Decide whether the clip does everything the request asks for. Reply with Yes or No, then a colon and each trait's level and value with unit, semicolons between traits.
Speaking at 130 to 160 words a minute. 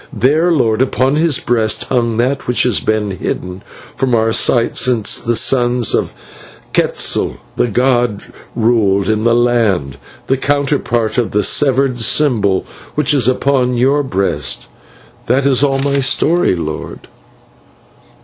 Yes: average, 140 wpm